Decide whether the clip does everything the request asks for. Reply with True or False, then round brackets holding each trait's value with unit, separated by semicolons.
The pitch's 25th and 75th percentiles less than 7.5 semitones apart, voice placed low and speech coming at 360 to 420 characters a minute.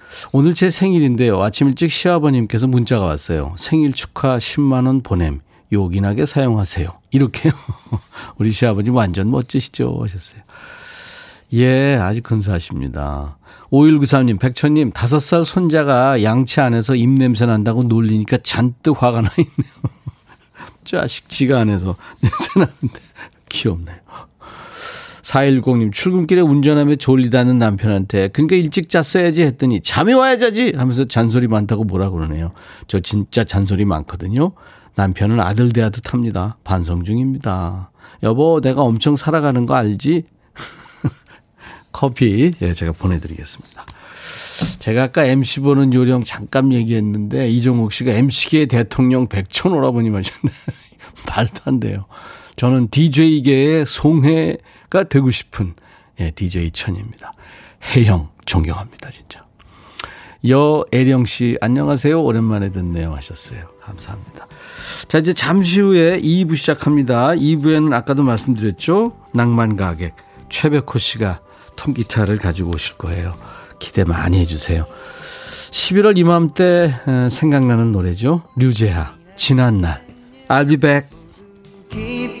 False (6.6 semitones; 125 Hz; 290 characters per minute)